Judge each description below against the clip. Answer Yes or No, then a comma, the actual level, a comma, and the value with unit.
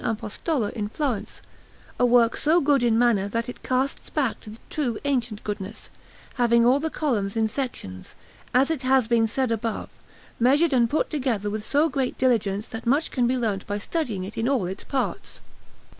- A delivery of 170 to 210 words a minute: Yes, average, 190 wpm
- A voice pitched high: Yes, high, 240 Hz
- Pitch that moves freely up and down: No, average, 3.9 semitones